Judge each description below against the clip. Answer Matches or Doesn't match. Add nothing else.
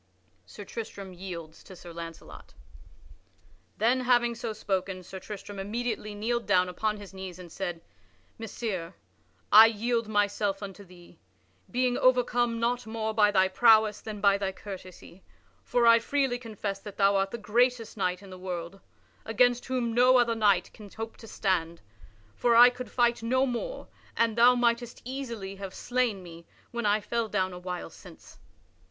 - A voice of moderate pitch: Doesn't match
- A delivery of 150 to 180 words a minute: Matches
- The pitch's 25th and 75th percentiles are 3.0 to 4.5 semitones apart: Matches